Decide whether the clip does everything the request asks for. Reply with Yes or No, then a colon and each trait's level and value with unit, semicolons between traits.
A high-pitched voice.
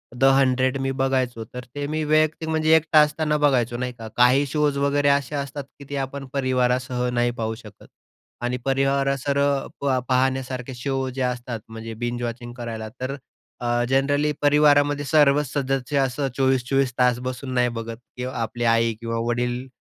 No: low, 130 Hz